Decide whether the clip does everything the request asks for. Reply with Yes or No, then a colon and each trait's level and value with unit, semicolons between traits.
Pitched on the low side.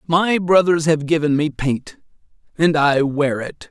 No: medium, 155 Hz